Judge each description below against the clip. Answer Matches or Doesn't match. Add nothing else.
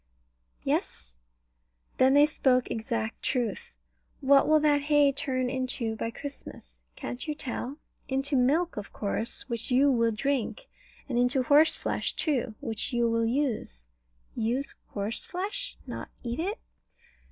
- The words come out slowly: Matches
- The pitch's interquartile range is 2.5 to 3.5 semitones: Doesn't match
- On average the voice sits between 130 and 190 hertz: Doesn't match